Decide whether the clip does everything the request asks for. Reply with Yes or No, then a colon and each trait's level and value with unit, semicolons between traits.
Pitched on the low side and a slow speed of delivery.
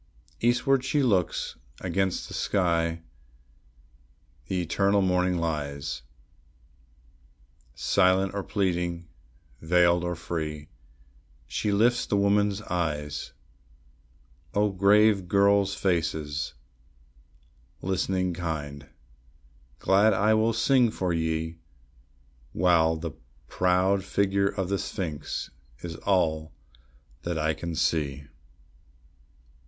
Yes: very low, 90 Hz; slow, 95 wpm